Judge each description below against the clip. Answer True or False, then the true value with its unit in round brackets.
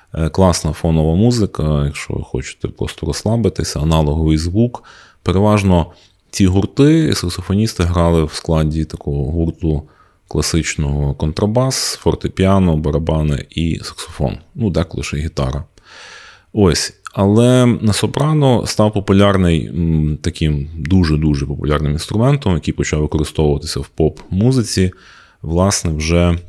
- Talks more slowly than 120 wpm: True (105 wpm)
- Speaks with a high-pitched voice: False (85 Hz)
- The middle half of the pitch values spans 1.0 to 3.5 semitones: False (4.5 semitones)